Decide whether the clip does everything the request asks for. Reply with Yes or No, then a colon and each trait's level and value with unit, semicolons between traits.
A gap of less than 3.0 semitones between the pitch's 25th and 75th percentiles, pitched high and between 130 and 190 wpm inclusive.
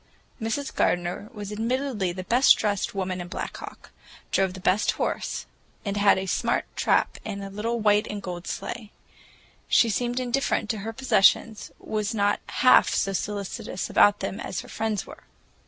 Yes: narrow, 2.6 semitones; high, 205 Hz; average, 170 wpm